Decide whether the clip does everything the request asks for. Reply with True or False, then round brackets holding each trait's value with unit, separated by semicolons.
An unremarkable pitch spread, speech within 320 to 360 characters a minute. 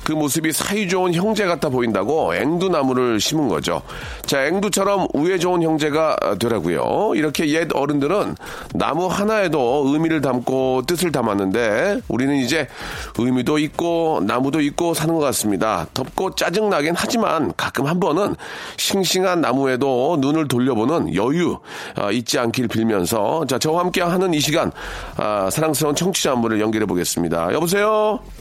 False (5.8 semitones; 335 characters per minute)